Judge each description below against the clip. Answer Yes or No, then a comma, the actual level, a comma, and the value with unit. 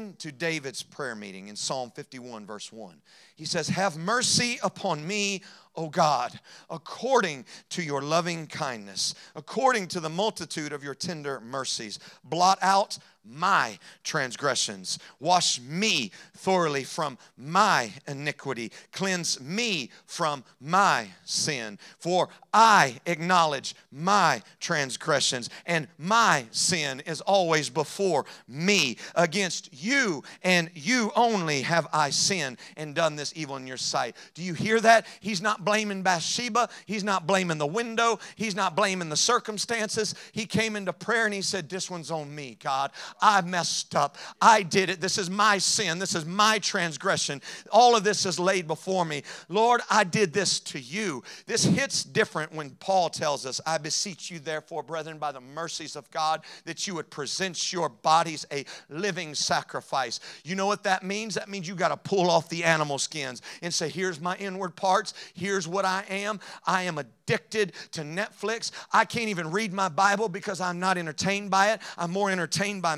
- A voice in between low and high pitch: Yes, medium, 180 Hz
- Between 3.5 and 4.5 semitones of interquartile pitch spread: Yes, average, 4.2 semitones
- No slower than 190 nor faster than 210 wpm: No, average, 165 wpm